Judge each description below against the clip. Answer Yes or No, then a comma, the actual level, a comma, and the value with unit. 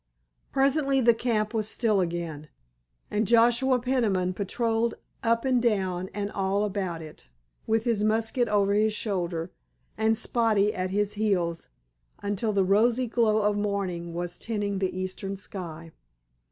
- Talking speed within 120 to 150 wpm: Yes, average, 140 wpm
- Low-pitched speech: No, high, 210 Hz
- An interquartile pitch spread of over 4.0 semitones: No, average, 3.4 semitones